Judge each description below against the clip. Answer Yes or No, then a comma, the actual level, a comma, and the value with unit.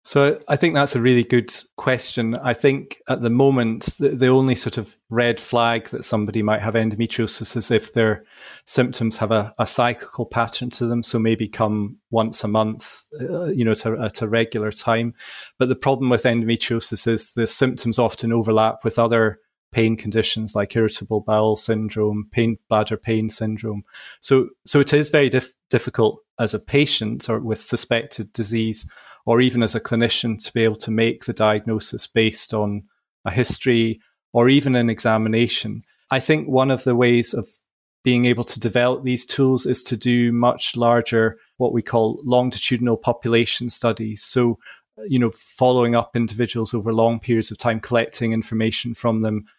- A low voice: Yes, low, 115 Hz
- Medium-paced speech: Yes, average, 175 wpm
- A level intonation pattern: Yes, narrow, 1.8 semitones